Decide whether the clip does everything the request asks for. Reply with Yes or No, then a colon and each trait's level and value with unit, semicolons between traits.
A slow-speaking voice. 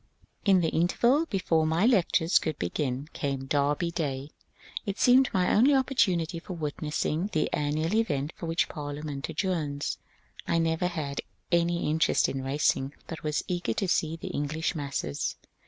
No: average, 155 wpm